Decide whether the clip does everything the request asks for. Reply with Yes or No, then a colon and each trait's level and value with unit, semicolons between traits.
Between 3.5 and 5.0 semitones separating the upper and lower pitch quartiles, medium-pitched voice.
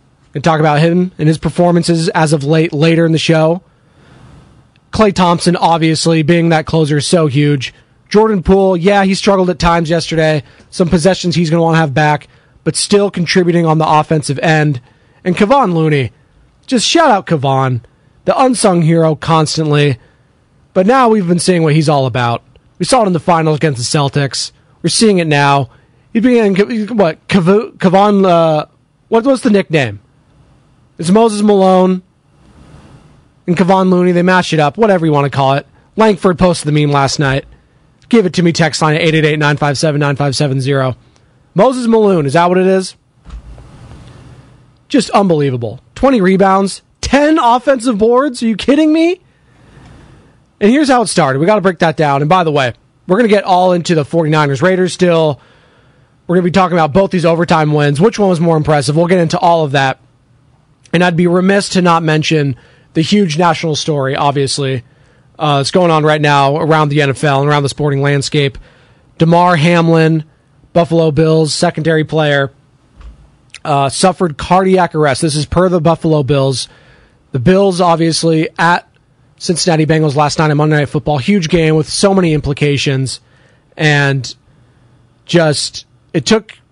Yes: average, 4.4 semitones; medium, 160 Hz